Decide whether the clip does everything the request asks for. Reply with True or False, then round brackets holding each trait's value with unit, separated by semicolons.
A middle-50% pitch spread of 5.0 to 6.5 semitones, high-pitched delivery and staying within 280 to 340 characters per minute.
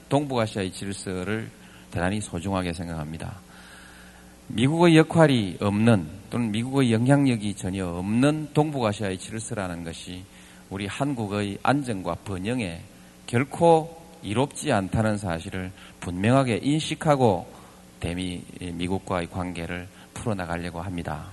False (5.4 semitones; 100 Hz; 285 characters per minute)